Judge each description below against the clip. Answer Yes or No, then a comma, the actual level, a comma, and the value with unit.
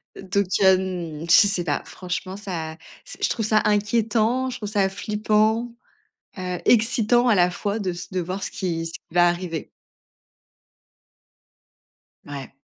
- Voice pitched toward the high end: Yes, high, 195 Hz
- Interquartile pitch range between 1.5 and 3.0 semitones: No, average, 3.4 semitones